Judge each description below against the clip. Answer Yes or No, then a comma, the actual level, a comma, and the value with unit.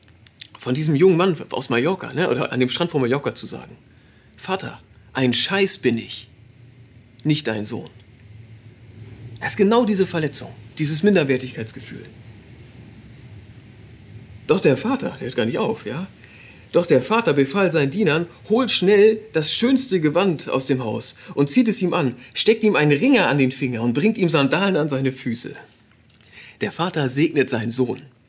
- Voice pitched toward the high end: No, low, 130 Hz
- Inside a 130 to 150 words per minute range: No, average, 160 wpm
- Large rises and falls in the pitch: Yes, wide, 7.1 semitones